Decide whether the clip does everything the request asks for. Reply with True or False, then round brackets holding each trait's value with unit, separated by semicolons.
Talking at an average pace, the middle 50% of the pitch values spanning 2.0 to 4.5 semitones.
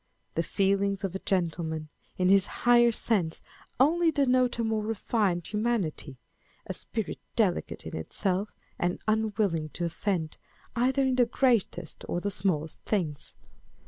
False (145 wpm; 5.2 semitones)